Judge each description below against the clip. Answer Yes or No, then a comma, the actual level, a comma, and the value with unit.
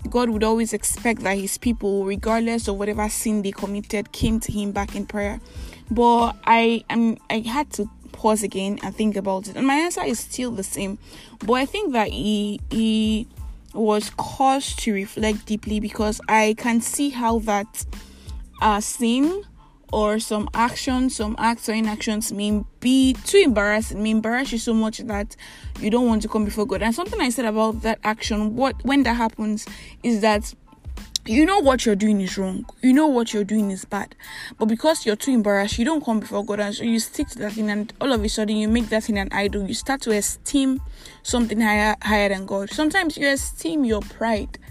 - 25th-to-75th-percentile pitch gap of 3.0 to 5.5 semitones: No, narrow, 2.4 semitones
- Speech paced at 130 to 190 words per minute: No, average, 200 wpm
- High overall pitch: Yes, high, 220 Hz